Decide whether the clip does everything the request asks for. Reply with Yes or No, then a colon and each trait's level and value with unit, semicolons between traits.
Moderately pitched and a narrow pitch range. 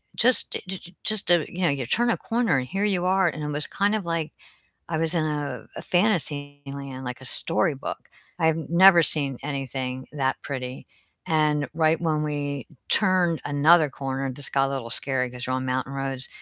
No: medium, 150 Hz; average, 4.1 semitones